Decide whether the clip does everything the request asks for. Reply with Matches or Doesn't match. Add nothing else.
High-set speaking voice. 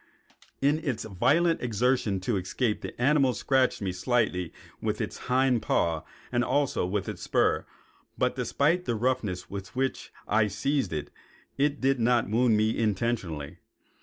Doesn't match